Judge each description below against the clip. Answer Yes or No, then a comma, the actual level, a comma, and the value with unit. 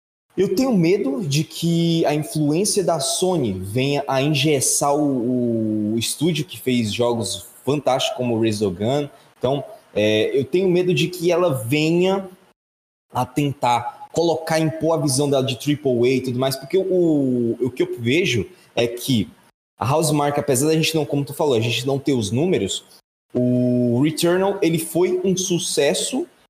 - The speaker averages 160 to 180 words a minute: Yes, average, 170 wpm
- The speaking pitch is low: No, medium, 145 Hz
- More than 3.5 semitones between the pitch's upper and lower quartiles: Yes, average, 5.3 semitones